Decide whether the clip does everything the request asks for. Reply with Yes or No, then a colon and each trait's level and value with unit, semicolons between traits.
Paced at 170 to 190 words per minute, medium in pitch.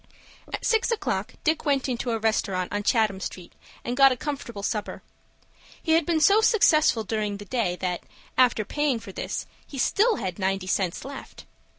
No: average, 180 wpm; high, 235 Hz